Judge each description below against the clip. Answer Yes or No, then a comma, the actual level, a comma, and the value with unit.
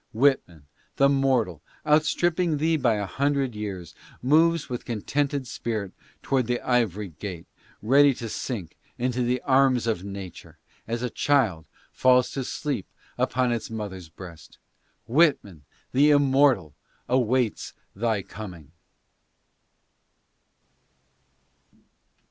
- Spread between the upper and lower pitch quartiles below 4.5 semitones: No, wide, 5.4 semitones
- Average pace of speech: No, slow, 110 wpm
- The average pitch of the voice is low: Yes, low, 120 Hz